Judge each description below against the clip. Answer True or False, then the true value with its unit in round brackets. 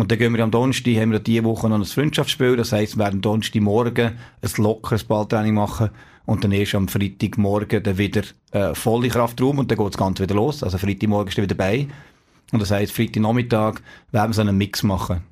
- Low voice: True (110 Hz)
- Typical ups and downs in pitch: False (2.3 semitones)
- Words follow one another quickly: True (215 wpm)